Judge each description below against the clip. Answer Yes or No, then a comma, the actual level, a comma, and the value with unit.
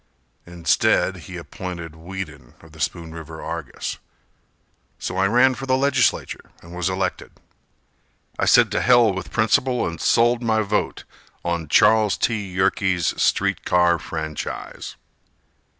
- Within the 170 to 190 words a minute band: No, slow, 135 wpm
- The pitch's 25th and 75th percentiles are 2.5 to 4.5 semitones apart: No, average, 5.0 semitones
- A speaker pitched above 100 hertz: No, very low, 90 Hz